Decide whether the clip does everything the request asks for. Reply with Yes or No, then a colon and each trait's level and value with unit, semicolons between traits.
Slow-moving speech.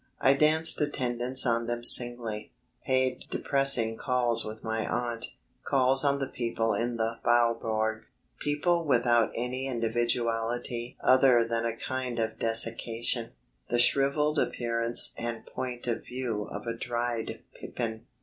Yes: slow, 130 wpm